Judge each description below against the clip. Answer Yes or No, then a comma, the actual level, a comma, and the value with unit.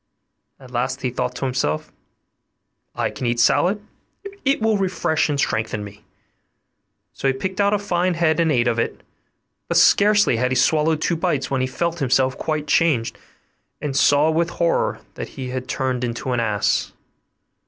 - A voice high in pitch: No, low, 135 Hz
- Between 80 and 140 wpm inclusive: No, average, 175 wpm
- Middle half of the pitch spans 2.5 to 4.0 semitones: No, average, 5.2 semitones